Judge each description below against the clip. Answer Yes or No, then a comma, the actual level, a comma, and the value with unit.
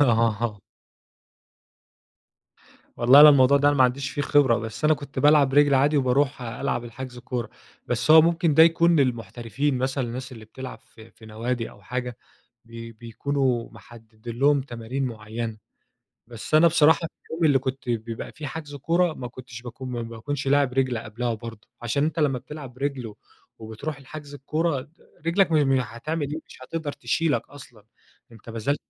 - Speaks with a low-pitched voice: Yes, low, 130 Hz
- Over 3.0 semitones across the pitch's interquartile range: Yes, average, 3.7 semitones